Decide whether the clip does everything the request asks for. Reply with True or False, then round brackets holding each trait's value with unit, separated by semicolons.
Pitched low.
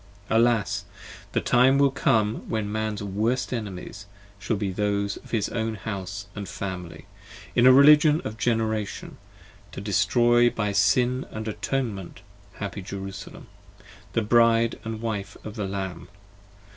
True (110 Hz)